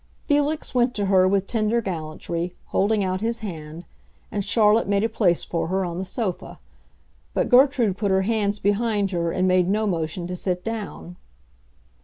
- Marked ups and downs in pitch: No, average, 3.6 semitones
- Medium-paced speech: Yes, average, 175 wpm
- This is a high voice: Yes, high, 200 Hz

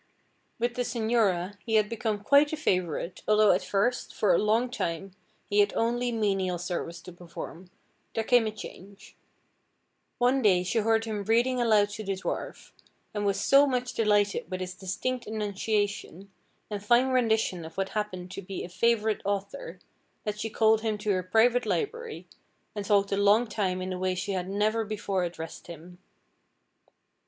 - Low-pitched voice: No, high, 210 Hz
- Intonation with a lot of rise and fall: No, average, 3.3 semitones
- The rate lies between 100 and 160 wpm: No, average, 175 wpm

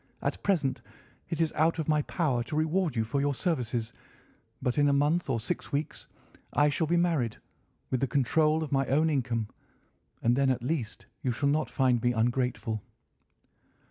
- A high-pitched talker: No, medium, 140 Hz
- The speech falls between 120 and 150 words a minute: No, average, 180 wpm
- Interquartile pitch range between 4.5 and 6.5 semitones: No, average, 4.1 semitones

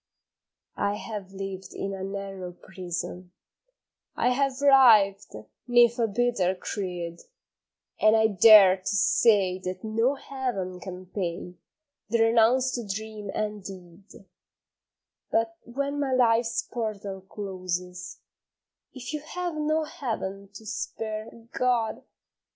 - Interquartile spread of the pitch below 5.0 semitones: Yes, average, 4.2 semitones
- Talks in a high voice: Yes, high, 210 Hz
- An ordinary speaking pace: No, slow, 115 wpm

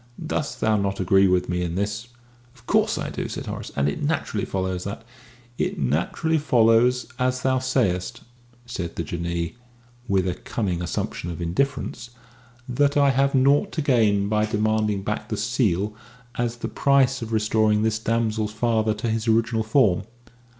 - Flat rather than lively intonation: No, average, 4.3 semitones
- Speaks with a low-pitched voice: Yes, low, 110 Hz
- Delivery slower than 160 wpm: No, average, 170 wpm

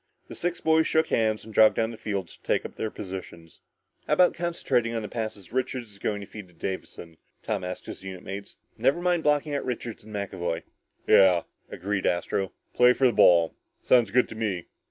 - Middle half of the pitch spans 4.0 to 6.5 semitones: Yes, average, 4.8 semitones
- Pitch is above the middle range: No, low, 110 Hz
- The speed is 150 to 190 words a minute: No, fast, 205 wpm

